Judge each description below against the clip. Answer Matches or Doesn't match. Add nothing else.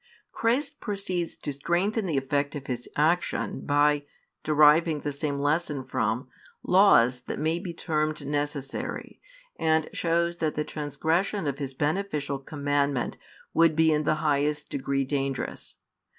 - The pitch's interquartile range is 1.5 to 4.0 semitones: Matches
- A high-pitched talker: Doesn't match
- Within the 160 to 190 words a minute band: Doesn't match